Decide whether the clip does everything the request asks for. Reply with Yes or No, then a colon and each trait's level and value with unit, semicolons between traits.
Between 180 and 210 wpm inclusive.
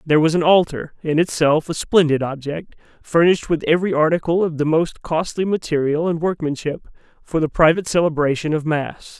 No: average, 170 wpm